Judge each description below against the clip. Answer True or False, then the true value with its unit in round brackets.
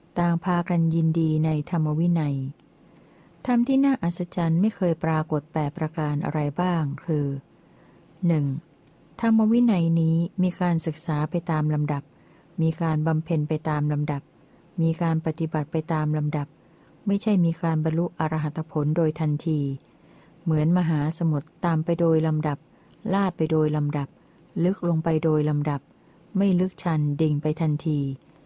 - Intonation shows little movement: True (2.0 semitones)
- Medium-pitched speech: True (160 Hz)